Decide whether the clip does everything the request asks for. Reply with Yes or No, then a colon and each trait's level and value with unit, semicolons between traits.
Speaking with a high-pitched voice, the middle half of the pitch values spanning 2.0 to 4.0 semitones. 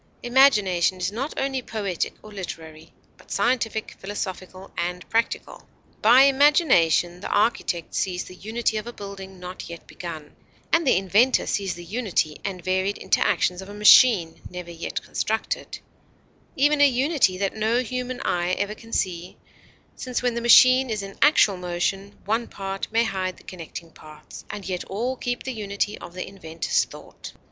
No: high, 200 Hz; average, 4.8 semitones